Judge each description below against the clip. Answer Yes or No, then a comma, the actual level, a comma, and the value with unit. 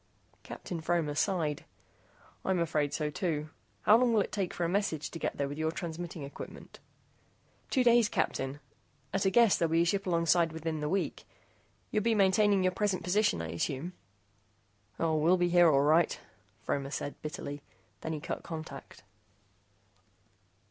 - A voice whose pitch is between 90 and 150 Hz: No, medium, 170 Hz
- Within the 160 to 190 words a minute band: Yes, average, 165 wpm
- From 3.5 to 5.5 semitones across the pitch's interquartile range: Yes, average, 3.9 semitones